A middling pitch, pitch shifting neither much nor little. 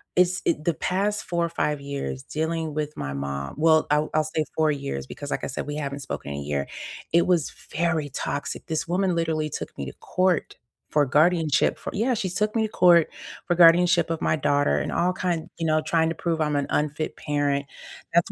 Yes: medium, 160 Hz; average, 3.0 semitones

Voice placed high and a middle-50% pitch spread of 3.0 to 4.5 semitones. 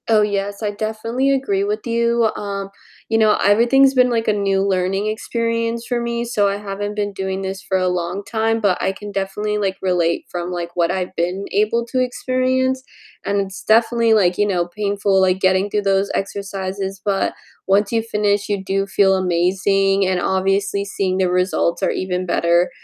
No: high, 200 Hz; narrow, 2.4 semitones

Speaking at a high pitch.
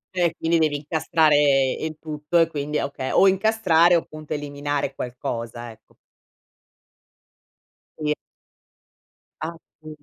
No: medium, 150 Hz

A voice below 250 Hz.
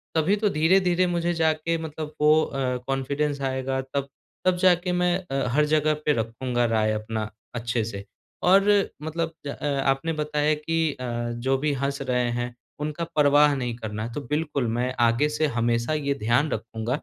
Yes: medium, 140 Hz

